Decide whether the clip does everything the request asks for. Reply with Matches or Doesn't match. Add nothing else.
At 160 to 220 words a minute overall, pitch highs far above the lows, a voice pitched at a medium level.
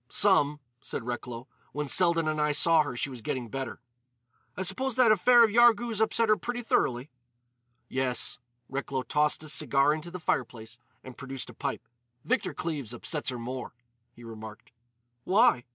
Matches